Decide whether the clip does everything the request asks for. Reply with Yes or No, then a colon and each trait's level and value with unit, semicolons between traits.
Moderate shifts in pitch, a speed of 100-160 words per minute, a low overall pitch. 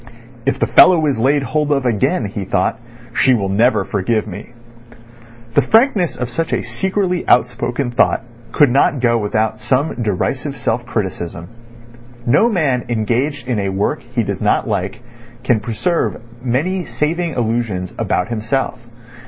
Yes: average, 5.0 semitones; average, 150 wpm; low, 125 Hz